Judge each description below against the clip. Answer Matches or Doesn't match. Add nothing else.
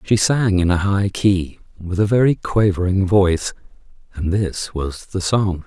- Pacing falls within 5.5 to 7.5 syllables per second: Doesn't match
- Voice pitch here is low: Matches